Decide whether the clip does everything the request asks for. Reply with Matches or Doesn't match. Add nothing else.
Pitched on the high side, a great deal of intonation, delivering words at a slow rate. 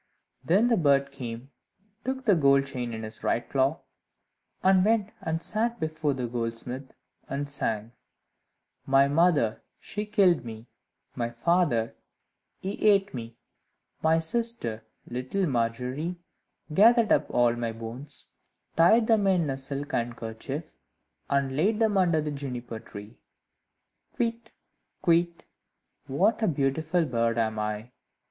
Doesn't match